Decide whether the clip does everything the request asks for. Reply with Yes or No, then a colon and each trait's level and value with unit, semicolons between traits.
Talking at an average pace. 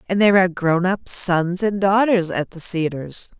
Yes: average, 195 wpm